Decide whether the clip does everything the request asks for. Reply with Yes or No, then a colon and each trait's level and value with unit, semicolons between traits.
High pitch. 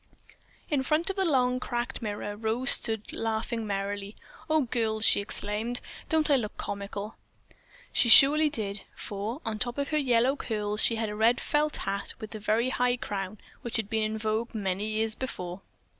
Yes: high, 225 Hz